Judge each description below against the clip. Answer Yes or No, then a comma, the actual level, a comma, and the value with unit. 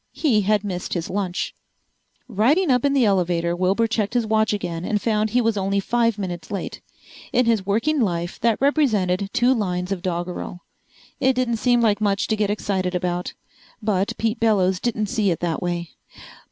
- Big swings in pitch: No, average, 4.1 semitones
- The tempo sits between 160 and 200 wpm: Yes, average, 180 wpm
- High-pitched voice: Yes, high, 205 Hz